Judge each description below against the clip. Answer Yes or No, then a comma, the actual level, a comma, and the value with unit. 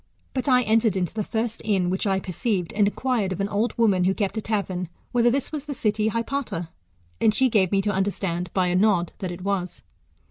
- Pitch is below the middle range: No, high, 205 Hz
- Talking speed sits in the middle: No, fast, 220 wpm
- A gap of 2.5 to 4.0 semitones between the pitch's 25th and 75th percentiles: Yes, average, 3.6 semitones